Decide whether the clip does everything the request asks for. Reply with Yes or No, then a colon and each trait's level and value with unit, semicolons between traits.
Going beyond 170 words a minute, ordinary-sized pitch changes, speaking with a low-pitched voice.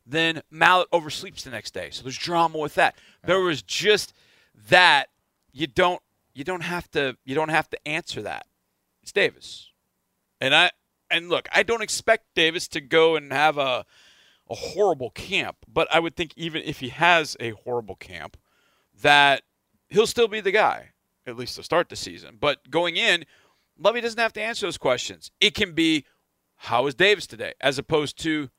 No: average, 185 wpm; average, 4.0 semitones; medium, 160 Hz